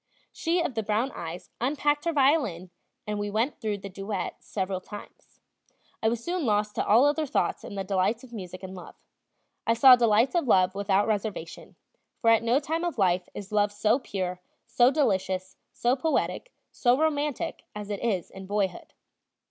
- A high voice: Yes, high, 215 Hz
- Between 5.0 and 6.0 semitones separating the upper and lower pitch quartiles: Yes, wide, 5.4 semitones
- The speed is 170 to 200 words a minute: Yes, average, 180 wpm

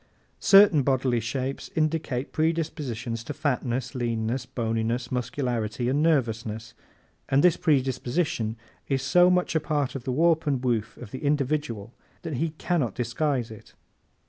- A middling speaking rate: Yes, average, 145 wpm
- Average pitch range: Yes, average, 4.4 semitones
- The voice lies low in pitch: Yes, low, 130 Hz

